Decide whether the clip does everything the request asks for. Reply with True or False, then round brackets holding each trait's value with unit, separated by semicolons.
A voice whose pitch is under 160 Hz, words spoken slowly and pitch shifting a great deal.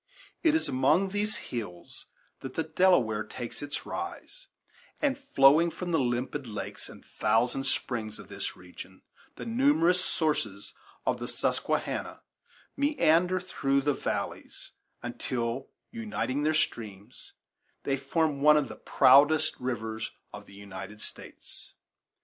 True (140 Hz; 130 wpm; 7.1 semitones)